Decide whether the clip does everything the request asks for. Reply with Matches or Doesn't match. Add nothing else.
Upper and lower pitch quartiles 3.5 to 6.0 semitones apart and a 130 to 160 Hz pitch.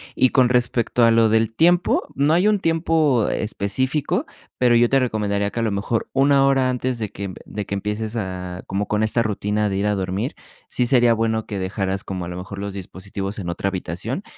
Doesn't match